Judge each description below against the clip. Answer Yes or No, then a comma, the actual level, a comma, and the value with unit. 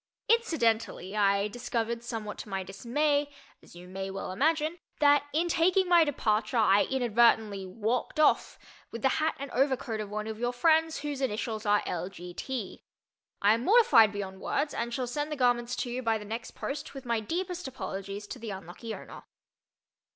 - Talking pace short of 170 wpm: No, average, 180 wpm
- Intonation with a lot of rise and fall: Yes, wide, 5.7 semitones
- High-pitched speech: Yes, high, 235 Hz